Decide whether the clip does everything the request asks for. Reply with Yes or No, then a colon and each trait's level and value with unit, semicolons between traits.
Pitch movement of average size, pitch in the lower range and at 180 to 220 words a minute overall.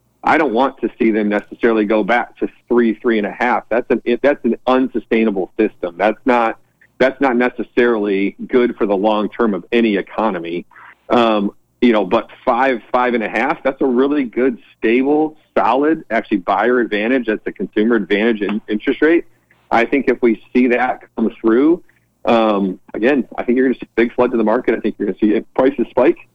Yes: average, 3.0 semitones; low, 120 Hz; fast, 205 wpm